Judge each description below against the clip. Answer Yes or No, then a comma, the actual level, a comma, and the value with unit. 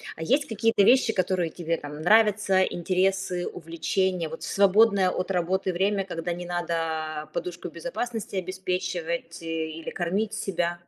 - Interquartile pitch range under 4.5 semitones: Yes, average, 2.7 semitones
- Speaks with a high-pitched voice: No, medium, 180 Hz